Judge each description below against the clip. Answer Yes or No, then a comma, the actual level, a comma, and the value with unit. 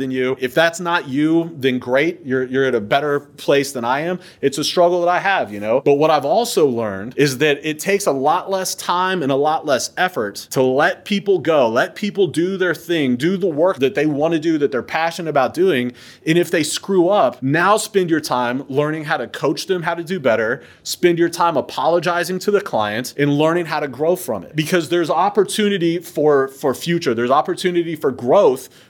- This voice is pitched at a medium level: Yes, medium, 160 Hz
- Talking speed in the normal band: No, fast, 220 wpm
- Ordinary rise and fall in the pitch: Yes, average, 4.3 semitones